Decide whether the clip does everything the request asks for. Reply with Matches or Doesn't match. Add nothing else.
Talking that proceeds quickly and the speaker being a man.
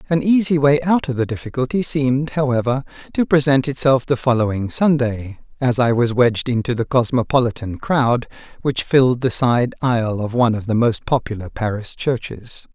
Doesn't match